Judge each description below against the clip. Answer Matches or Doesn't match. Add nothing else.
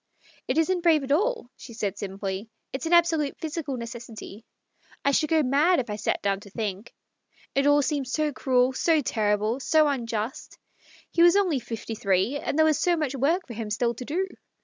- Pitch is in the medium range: Doesn't match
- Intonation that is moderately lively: Doesn't match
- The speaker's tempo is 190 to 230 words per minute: Matches